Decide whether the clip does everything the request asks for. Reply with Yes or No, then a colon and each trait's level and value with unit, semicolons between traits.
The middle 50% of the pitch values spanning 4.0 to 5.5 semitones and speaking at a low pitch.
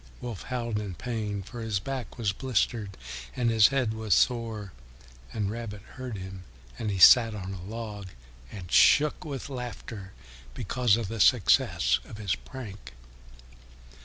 No: average, 3.6 semitones; low, 110 Hz